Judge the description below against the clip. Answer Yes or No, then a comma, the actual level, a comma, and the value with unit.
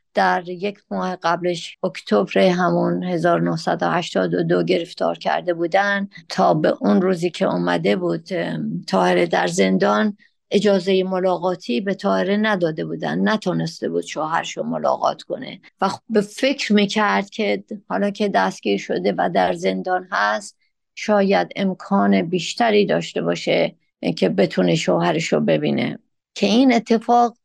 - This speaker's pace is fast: No, average, 130 wpm